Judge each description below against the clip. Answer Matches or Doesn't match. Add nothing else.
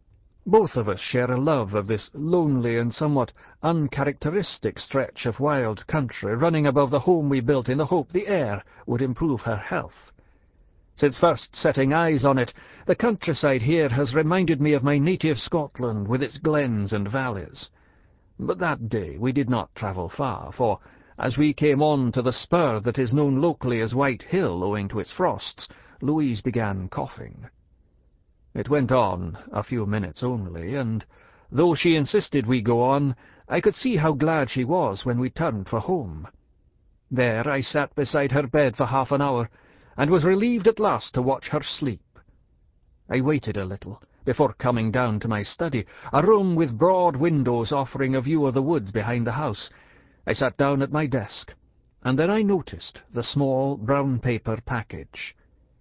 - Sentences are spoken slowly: Doesn't match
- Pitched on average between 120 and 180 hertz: Matches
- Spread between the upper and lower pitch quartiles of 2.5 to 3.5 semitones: Doesn't match